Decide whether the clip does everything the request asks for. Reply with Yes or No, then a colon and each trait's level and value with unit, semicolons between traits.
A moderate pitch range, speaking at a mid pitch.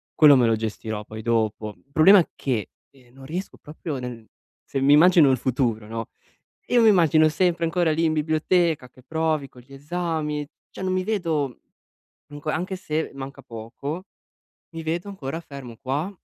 Yes: average, 4.6 semitones; medium, 150 Hz